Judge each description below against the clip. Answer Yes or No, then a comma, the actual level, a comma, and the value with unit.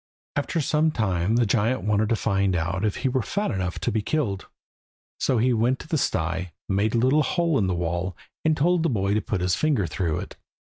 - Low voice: Yes, low, 110 Hz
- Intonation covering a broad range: Yes, wide, 6.3 semitones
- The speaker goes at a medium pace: No, fast, 225 wpm